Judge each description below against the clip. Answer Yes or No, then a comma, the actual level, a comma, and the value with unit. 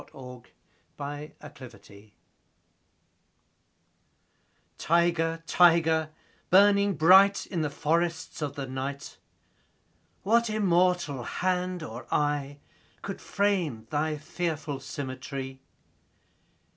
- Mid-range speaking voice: Yes, medium, 155 Hz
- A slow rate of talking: Yes, slow, 80 wpm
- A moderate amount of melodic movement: Yes, average, 4.3 semitones